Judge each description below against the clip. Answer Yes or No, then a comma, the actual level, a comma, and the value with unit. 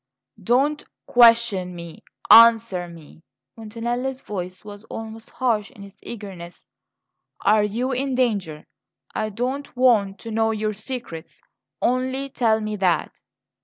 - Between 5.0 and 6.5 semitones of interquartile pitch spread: No, average, 3.8 semitones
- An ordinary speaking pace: No, slow, 125 wpm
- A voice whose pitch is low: No, high, 220 Hz